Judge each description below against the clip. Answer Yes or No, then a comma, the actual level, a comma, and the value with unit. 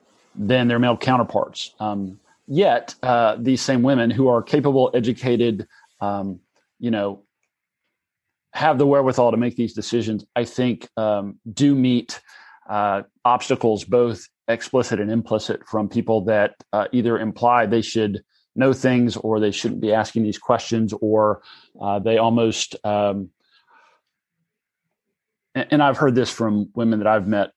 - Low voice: Yes, low, 115 Hz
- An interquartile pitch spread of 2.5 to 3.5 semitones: Yes, average, 2.9 semitones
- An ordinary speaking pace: Yes, average, 145 wpm